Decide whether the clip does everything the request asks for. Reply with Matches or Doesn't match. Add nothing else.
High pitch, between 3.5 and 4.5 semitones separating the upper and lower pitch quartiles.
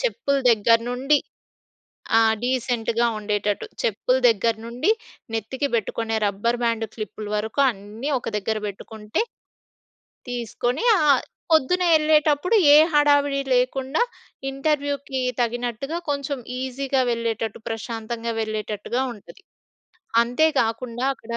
Matches